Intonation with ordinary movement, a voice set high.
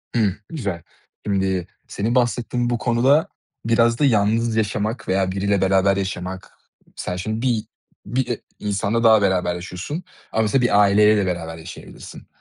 No: average, 3.4 semitones; low, 105 Hz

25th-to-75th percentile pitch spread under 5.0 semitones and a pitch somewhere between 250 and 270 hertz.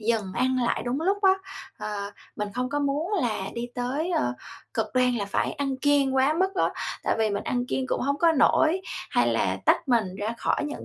Yes: average, 4.4 semitones; very high, 260 Hz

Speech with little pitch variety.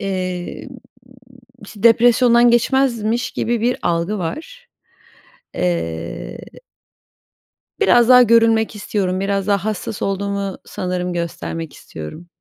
No: average, 4.6 semitones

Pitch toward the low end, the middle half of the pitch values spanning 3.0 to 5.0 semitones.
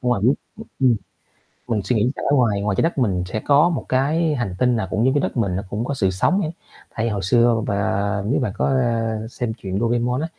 Yes: low, 115 Hz; average, 4.2 semitones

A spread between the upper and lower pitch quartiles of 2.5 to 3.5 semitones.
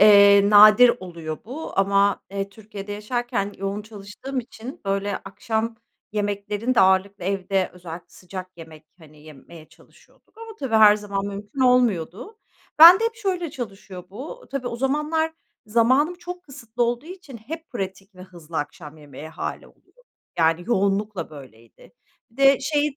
No: average, 5.3 semitones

